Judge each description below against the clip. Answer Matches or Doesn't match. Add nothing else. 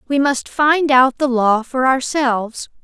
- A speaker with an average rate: Matches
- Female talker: Matches